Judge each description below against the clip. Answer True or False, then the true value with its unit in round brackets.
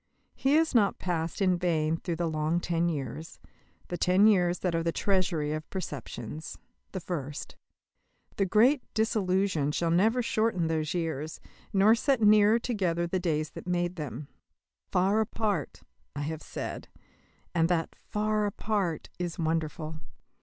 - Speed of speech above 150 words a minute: False (145 wpm)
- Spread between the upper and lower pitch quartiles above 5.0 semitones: False (4.3 semitones)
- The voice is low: False (175 Hz)